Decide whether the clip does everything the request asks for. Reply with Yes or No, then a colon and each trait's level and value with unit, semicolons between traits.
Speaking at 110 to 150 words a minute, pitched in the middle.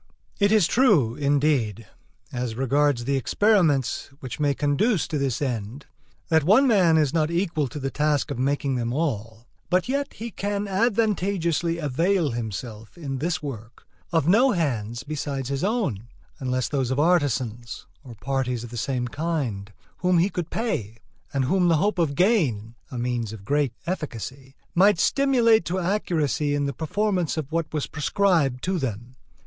No: average, 165 wpm; medium, 145 Hz